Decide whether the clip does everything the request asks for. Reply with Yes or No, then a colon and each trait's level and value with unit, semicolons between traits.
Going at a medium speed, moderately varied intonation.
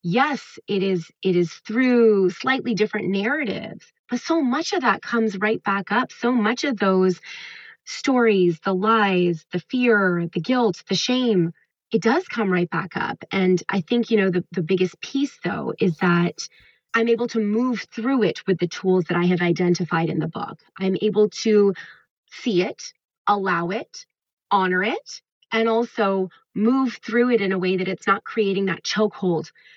Yes: average, 175 wpm; average, 4.1 semitones